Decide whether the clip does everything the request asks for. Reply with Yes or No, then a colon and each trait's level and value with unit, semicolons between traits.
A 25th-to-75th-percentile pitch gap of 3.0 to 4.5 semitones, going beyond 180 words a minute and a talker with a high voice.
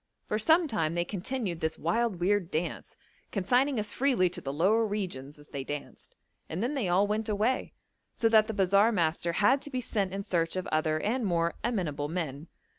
No: average, 5.0 semitones; average, 195 wpm; high, 195 Hz